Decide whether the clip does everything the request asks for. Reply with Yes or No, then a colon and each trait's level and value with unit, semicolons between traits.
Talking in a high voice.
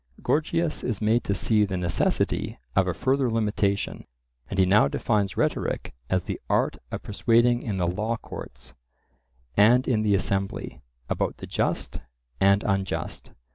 No: low, 105 Hz